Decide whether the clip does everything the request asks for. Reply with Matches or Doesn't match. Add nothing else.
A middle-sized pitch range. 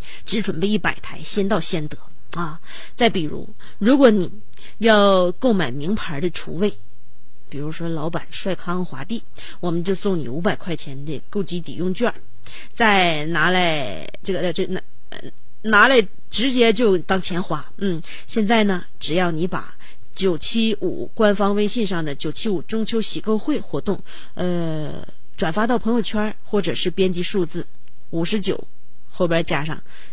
Matches